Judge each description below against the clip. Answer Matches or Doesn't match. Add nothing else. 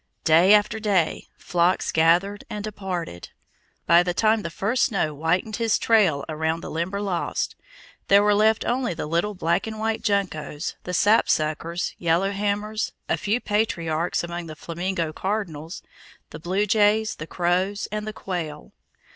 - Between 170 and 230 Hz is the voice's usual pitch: Matches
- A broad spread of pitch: Doesn't match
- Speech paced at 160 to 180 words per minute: Doesn't match